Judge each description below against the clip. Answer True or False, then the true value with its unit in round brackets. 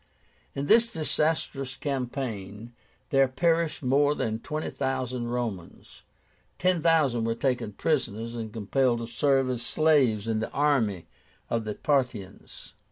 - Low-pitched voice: True (130 Hz)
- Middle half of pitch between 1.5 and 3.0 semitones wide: False (4.1 semitones)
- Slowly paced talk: True (130 wpm)